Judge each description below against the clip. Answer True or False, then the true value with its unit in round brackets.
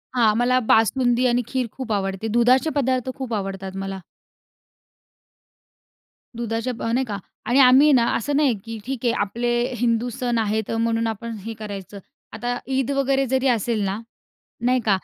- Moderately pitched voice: False (235 Hz)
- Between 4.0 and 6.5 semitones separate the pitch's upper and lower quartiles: False (2.8 semitones)